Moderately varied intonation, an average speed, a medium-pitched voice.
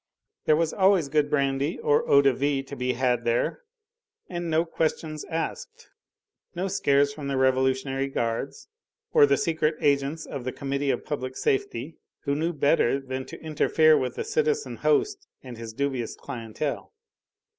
Yes: average, 4.0 semitones; average, 160 wpm; medium, 145 Hz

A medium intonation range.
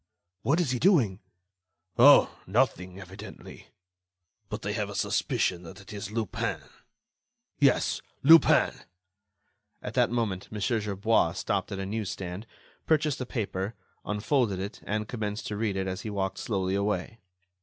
Yes: average, 3.1 semitones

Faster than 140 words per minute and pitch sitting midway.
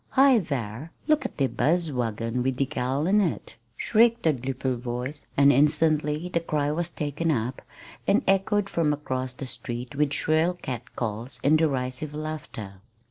Yes: average, 160 wpm; medium, 145 Hz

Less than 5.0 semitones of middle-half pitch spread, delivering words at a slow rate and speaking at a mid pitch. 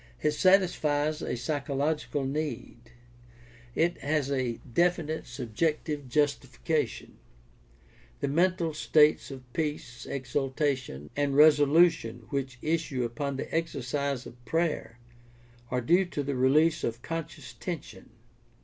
Yes: average, 3.5 semitones; slow, 110 wpm; medium, 145 Hz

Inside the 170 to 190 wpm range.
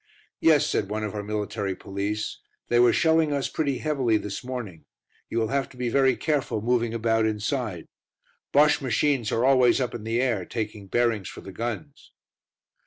Yes: average, 175 wpm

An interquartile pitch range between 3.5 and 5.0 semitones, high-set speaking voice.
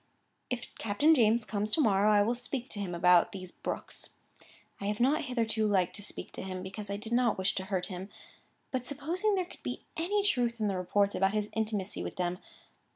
Yes: average, 4.2 semitones; high, 210 Hz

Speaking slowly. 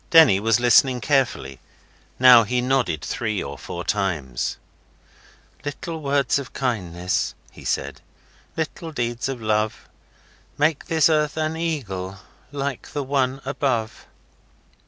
Yes: slow, 120 wpm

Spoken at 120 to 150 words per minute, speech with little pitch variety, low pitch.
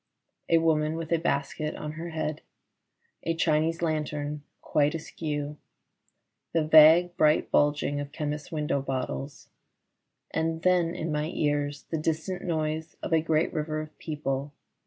No: average, 140 wpm; narrow, 1.7 semitones; medium, 155 Hz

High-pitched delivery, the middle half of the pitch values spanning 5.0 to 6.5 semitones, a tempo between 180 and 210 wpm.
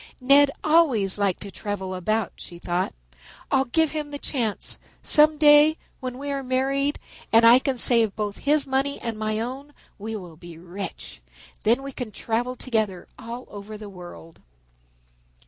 No: high, 235 Hz; average, 5.3 semitones; average, 165 wpm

